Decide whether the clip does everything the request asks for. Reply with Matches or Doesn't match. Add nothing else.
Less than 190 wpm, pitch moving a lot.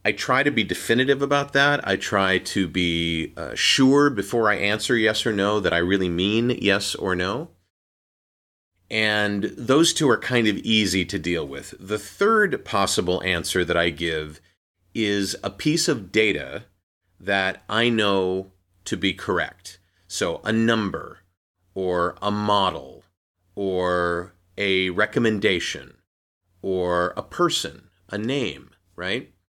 Doesn't match